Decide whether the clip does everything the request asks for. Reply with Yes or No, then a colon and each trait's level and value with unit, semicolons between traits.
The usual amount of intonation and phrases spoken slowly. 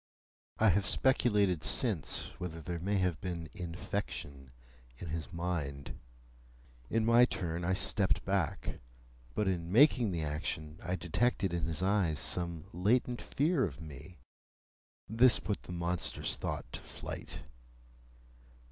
Yes: average, 3.8 semitones; slow, 130 wpm